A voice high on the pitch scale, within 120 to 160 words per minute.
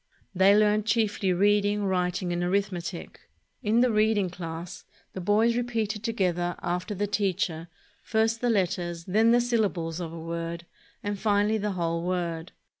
Yes: high, 195 Hz; average, 150 wpm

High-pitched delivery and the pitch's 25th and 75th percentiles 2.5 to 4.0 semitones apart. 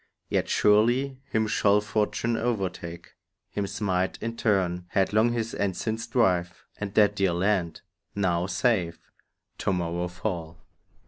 No: low, 100 Hz; average, 3.7 semitones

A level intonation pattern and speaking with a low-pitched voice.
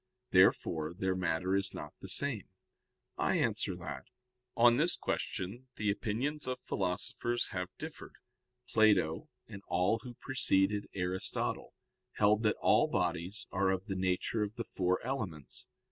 No: average, 3.8 semitones; low, 100 Hz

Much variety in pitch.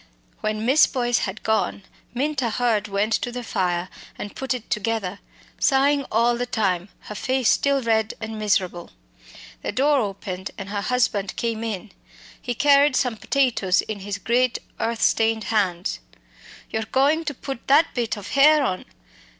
No: average, 4.0 semitones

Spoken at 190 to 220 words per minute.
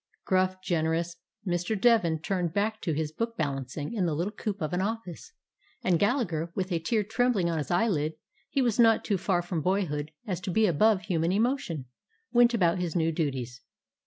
Yes: average, 195 wpm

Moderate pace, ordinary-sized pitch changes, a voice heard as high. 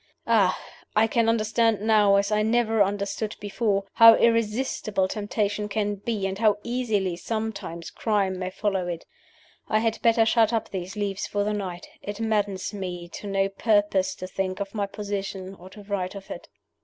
No: average, 175 wpm; narrow, 2.2 semitones; high, 205 Hz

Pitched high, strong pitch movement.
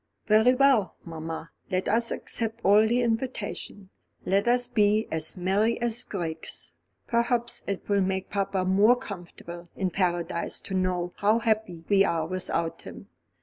No: high, 200 Hz; average, 4.1 semitones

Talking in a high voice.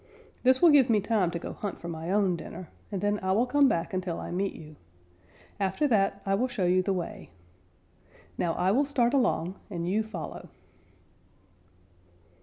Yes: high, 195 Hz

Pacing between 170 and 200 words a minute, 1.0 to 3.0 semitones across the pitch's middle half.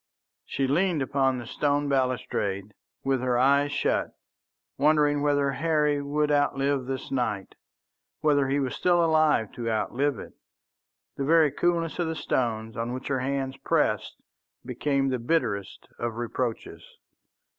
No: average, 140 wpm; average, 2.7 semitones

